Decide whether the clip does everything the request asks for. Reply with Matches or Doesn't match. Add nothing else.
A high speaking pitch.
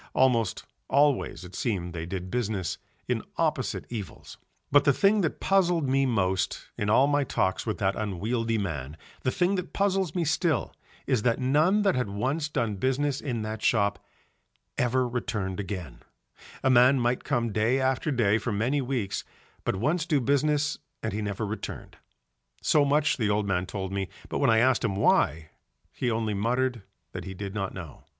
Doesn't match